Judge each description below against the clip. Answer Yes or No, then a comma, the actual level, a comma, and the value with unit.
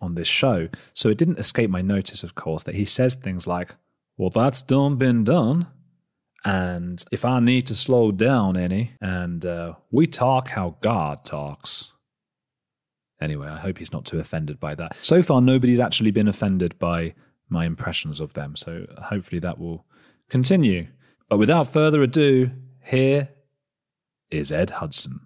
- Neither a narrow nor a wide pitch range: No, wide, 7.1 semitones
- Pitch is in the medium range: No, low, 105 Hz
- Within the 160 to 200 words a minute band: Yes, average, 165 wpm